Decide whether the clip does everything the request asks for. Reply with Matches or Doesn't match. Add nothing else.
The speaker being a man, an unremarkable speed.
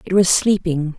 Doesn't match